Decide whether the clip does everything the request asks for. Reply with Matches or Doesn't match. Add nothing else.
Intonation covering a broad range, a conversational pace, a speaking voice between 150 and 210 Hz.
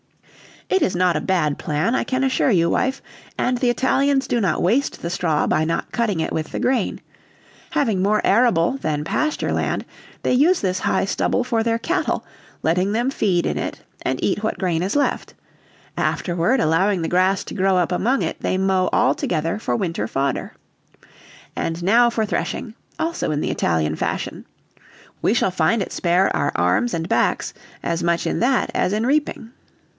Matches